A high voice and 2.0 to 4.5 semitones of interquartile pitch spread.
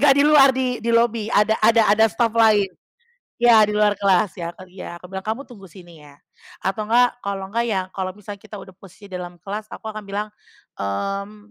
Yes: high, 210 Hz; average, 2.9 semitones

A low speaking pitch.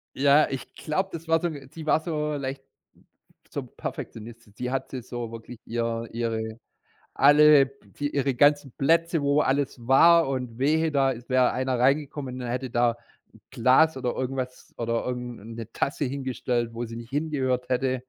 Yes: low, 130 Hz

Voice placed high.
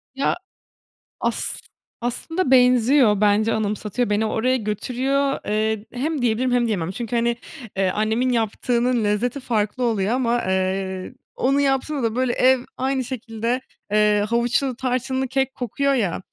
Yes: high, 240 Hz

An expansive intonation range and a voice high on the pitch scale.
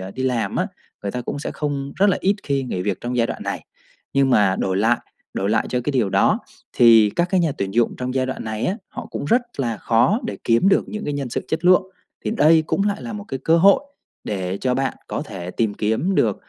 No: wide, 6.6 semitones; low, 130 Hz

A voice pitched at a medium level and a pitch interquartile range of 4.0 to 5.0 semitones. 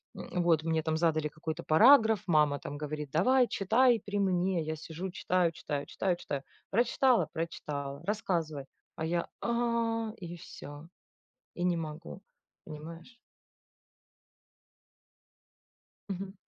Yes: medium, 170 Hz; average, 4.6 semitones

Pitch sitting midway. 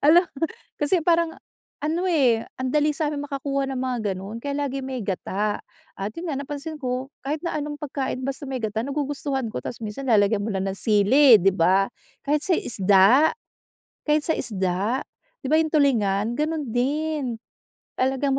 No: very high, 270 Hz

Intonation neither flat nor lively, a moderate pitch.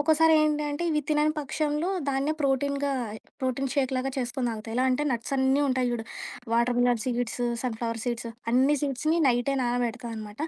No: average, 3.3 semitones; very high, 260 Hz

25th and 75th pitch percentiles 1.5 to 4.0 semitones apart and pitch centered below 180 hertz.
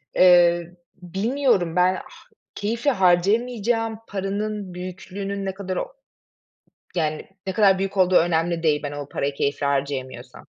No: average, 3.3 semitones; medium, 185 Hz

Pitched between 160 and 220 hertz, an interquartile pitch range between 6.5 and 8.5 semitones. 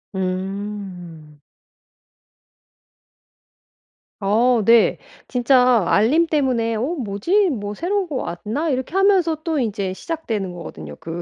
No: high, 230 Hz; wide, 7.7 semitones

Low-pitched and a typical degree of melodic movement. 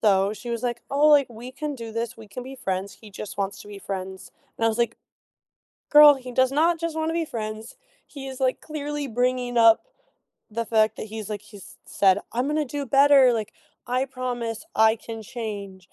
No: high, 235 Hz; average, 3.9 semitones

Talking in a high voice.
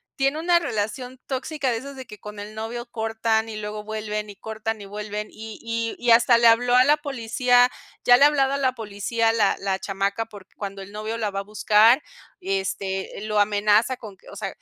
Yes: high, 220 Hz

